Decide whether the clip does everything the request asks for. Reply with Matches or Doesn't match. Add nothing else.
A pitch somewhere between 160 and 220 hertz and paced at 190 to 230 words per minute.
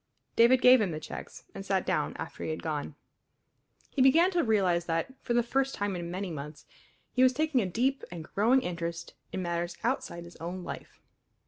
Matches